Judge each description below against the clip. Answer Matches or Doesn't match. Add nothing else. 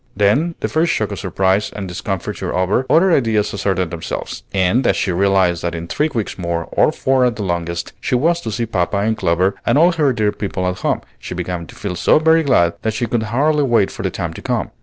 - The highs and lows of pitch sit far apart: Matches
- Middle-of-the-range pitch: Doesn't match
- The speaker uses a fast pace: Matches